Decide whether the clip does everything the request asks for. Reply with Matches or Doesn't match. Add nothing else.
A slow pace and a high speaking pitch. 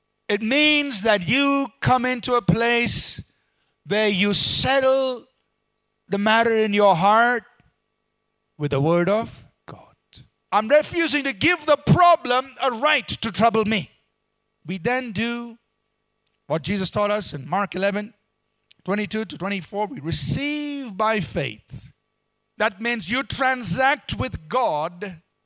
Matches